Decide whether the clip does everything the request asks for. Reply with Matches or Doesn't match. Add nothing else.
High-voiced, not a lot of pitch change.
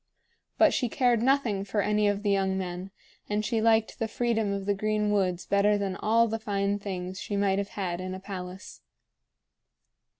Matches